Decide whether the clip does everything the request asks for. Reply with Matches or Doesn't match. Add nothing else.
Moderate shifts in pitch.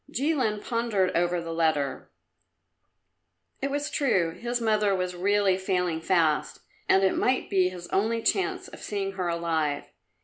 Matches